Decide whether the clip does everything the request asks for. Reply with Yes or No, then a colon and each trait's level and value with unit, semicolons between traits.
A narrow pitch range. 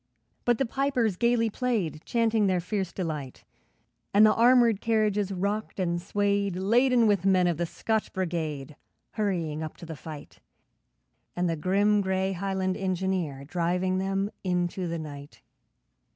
No: average, 3.6 semitones